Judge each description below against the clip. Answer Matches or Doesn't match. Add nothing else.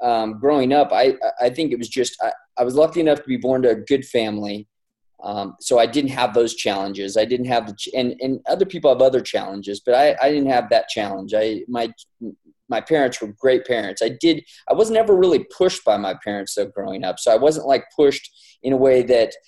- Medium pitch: Doesn't match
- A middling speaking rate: Doesn't match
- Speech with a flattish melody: Doesn't match